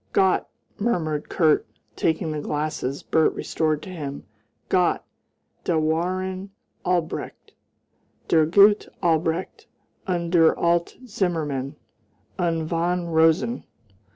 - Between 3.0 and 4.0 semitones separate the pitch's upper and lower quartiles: No, narrow, 2.6 semitones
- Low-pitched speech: No, medium, 165 Hz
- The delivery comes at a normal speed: No, slow, 100 wpm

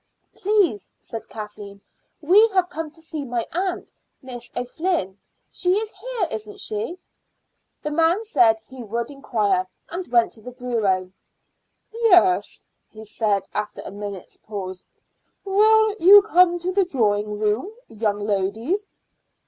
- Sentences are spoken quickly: No, slow, 135 wpm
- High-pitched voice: Yes, very high, 250 Hz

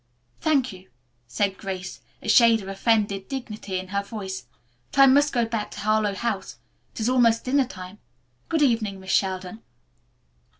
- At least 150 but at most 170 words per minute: Yes, average, 165 wpm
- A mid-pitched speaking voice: No, high, 215 Hz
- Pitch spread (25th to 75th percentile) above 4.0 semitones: No, average, 3.7 semitones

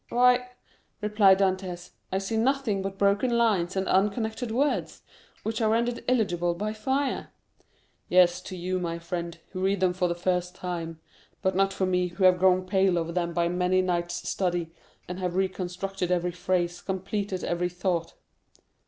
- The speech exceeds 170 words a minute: No, average, 165 wpm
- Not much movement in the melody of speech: Yes, narrow, 2.3 semitones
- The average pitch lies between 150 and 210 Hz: Yes, medium, 185 Hz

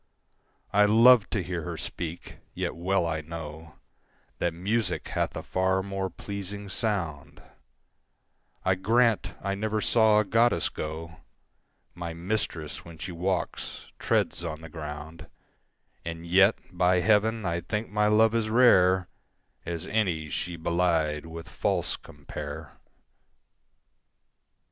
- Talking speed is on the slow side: Yes, slow, 125 wpm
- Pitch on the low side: Yes, very low, 90 Hz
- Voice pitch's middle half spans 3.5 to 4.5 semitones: Yes, average, 4.1 semitones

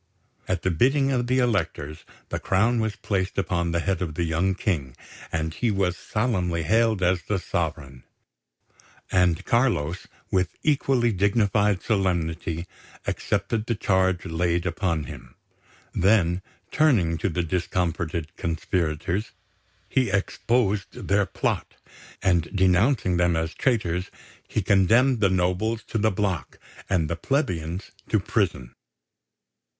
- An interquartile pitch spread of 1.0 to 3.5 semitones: No, average, 4.1 semitones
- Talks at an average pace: No, slow, 130 wpm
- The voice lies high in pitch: No, very low, 95 Hz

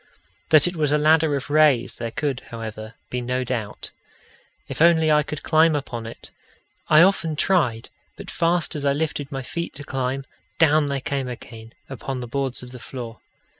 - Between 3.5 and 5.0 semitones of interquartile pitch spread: Yes, average, 3.8 semitones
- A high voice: No, medium, 140 Hz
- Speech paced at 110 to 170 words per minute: No, average, 185 wpm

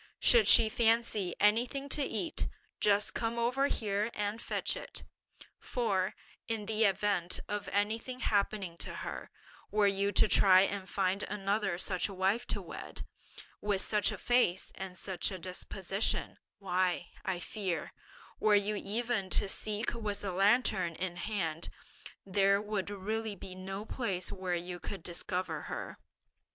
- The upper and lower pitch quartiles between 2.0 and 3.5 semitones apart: Yes, narrow, 2.6 semitones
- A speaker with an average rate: Yes, average, 150 wpm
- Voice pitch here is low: No, high, 200 Hz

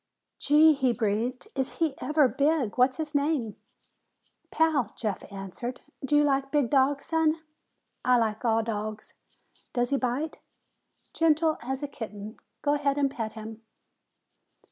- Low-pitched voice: No, very high, 265 Hz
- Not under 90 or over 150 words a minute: Yes, average, 145 wpm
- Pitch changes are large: No, average, 4.6 semitones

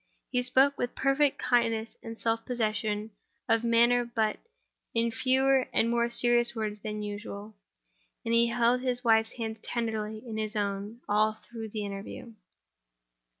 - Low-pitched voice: No, high, 230 Hz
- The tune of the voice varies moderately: No, narrow, 1.8 semitones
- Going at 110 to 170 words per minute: Yes, average, 145 wpm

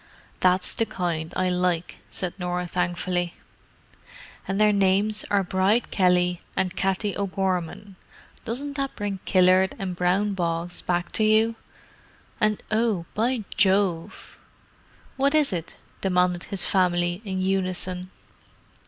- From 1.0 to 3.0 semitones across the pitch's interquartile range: Yes, narrow, 2.4 semitones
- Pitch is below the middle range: No, medium, 185 Hz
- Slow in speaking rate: Yes, slow, 120 wpm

